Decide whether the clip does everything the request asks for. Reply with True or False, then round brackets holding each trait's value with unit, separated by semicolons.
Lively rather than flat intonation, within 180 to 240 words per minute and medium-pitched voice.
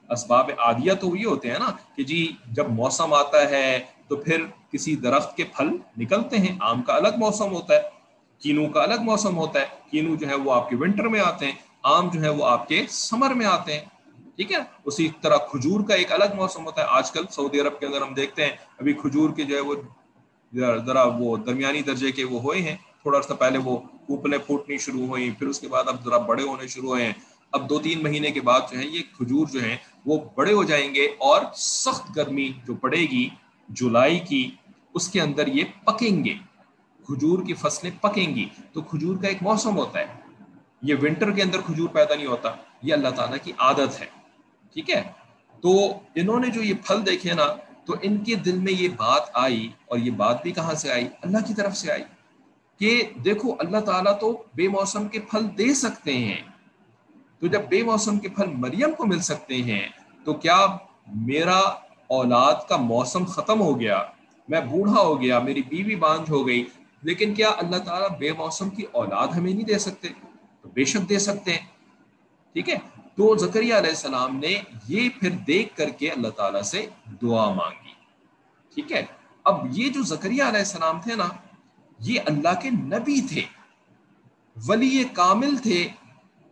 True (7.1 semitones; 200 wpm; 175 Hz)